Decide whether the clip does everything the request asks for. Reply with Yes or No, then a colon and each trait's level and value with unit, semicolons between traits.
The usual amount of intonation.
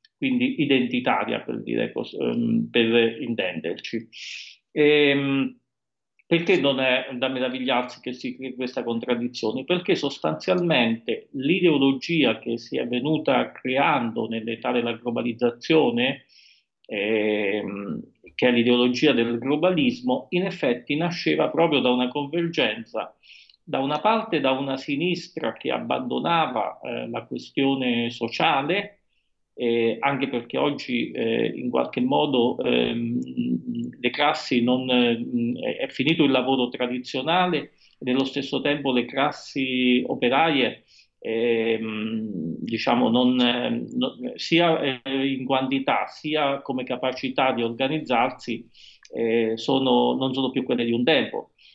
Yes: average, 4.1 semitones